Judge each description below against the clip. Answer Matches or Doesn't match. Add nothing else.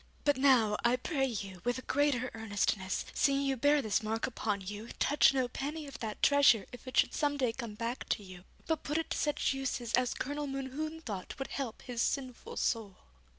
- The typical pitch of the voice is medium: Doesn't match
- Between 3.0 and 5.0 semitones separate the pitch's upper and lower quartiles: Matches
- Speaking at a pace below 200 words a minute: Doesn't match